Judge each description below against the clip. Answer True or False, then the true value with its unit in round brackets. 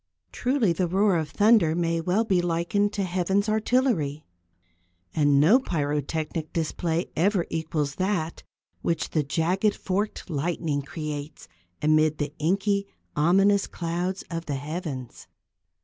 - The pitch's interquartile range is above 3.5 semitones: True (4.2 semitones)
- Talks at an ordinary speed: False (130 wpm)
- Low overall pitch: False (170 Hz)